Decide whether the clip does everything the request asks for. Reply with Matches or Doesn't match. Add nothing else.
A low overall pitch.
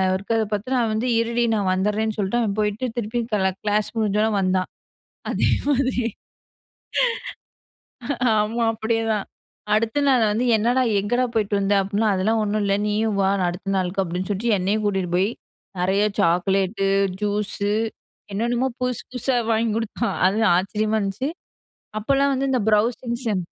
Doesn't match